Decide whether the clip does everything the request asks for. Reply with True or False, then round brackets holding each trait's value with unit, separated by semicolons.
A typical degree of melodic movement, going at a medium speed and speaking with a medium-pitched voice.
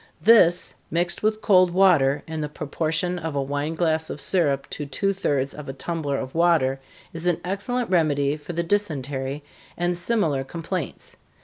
True (3.8 semitones; 170 wpm; 160 Hz)